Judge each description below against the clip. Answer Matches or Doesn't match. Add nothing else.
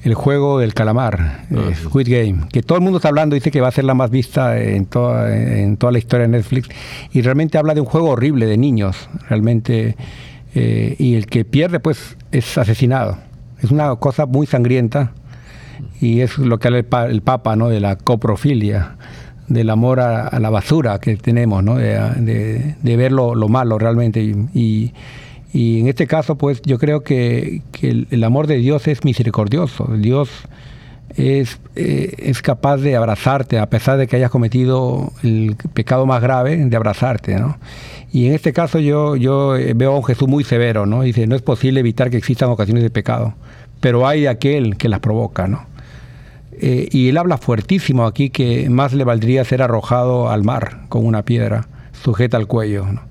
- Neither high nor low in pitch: Doesn't match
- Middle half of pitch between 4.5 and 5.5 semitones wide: Doesn't match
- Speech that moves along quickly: Matches